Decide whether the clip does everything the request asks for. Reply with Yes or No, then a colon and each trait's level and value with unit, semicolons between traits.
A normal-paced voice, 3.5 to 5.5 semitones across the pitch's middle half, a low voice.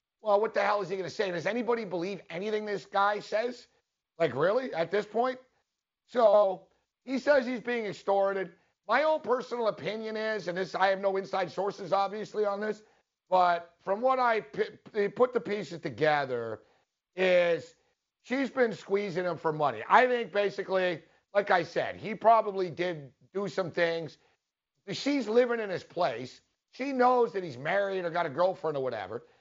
No: average, 175 wpm; average, 4.2 semitones; high, 200 Hz